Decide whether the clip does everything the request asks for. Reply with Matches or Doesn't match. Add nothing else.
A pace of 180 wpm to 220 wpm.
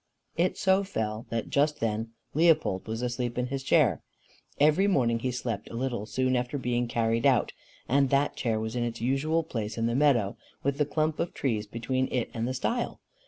Matches